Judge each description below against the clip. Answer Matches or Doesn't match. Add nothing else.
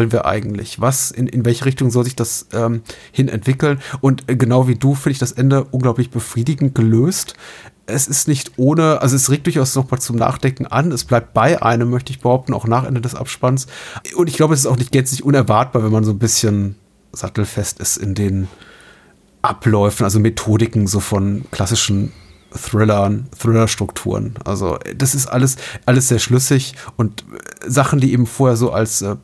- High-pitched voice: Doesn't match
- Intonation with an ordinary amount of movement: Matches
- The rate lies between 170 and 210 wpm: Matches